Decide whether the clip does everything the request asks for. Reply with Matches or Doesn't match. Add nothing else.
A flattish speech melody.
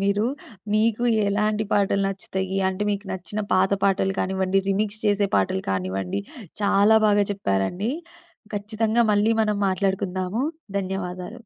Matches